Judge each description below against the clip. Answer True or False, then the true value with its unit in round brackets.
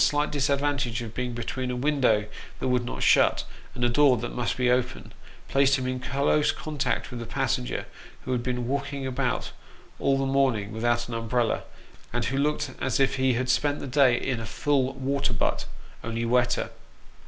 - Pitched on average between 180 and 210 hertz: False (130 Hz)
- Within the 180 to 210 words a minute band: True (190 wpm)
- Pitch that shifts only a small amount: True (2.3 semitones)